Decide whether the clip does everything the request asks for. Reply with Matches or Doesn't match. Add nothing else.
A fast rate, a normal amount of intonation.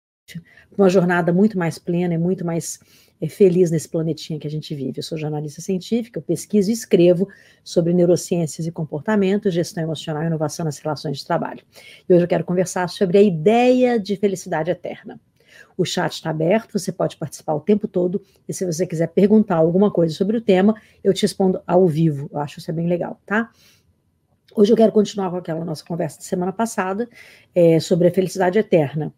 Matches